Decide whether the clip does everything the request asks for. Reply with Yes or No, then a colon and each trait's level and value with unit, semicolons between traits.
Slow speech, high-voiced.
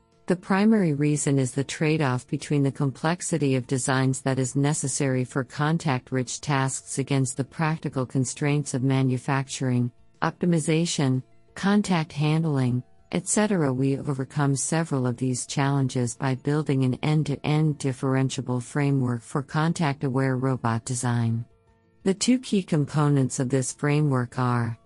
No: slow, 125 wpm; low, 135 Hz